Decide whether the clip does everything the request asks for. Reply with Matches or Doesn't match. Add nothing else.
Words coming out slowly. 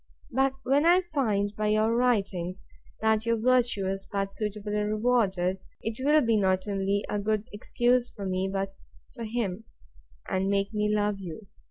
Doesn't match